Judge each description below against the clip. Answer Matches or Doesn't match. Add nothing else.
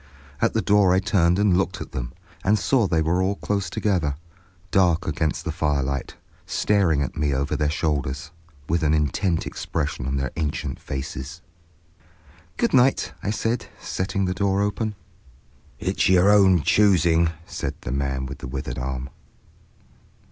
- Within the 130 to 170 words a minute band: Matches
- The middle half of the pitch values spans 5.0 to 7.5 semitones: Matches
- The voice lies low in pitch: Matches